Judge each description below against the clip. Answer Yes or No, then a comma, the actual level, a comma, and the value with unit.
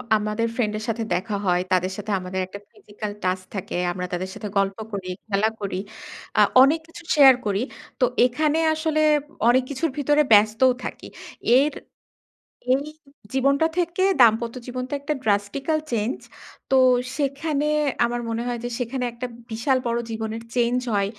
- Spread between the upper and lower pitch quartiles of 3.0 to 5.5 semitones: Yes, average, 4.8 semitones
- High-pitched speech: Yes, high, 235 Hz